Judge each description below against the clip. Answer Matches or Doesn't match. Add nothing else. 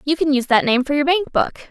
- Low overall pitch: Doesn't match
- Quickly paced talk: Matches